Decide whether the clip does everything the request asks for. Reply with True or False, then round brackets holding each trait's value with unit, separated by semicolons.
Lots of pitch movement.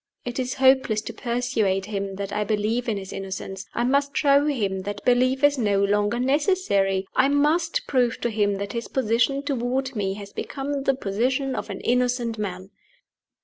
False (4.8 semitones)